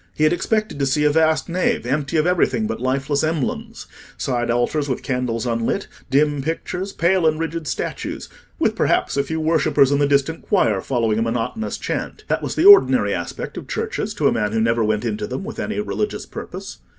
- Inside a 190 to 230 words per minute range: Yes, average, 195 wpm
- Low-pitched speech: No, medium, 145 Hz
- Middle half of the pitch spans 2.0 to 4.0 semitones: No, average, 5.3 semitones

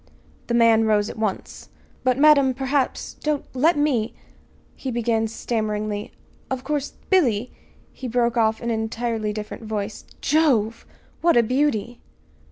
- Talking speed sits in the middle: Yes, average, 150 wpm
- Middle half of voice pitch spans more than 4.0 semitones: No, average, 3.5 semitones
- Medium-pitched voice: No, high, 235 Hz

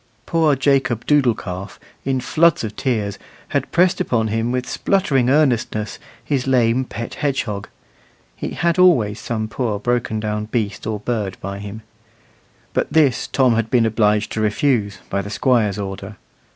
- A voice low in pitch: Yes, low, 115 Hz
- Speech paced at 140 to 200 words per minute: Yes, average, 155 wpm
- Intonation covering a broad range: No, average, 4.0 semitones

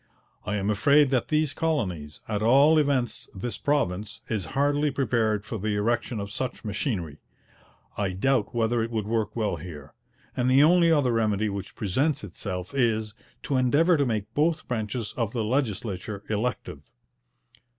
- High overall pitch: No, low, 115 Hz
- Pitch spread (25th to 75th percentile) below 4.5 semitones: No, average, 4.9 semitones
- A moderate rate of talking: Yes, average, 160 wpm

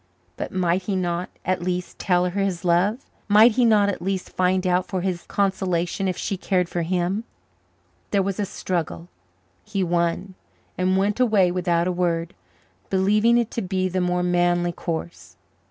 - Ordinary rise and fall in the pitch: No, narrow, 2.0 semitones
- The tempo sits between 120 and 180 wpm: Yes, average, 170 wpm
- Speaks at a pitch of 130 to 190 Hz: Yes, medium, 185 Hz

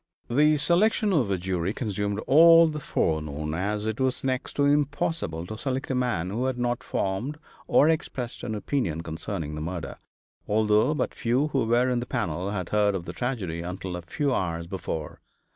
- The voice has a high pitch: No, low, 110 Hz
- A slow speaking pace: No, average, 185 wpm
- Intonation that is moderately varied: No, wide, 7.0 semitones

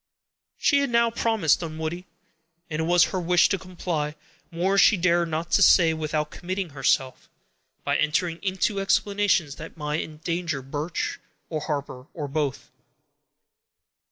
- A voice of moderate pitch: Yes, medium, 170 Hz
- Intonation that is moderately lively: Yes, average, 3.4 semitones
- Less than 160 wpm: Yes, slow, 135 wpm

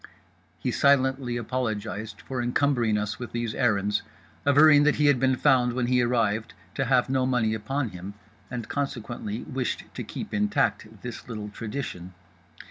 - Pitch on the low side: Yes, low, 125 Hz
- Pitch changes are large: No, average, 3.6 semitones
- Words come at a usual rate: Yes, average, 155 wpm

